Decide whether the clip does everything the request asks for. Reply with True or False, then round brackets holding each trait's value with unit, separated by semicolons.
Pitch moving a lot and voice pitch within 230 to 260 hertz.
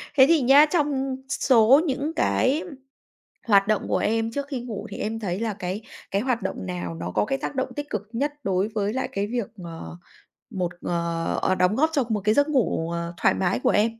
False (6.0 semitones; 220 Hz)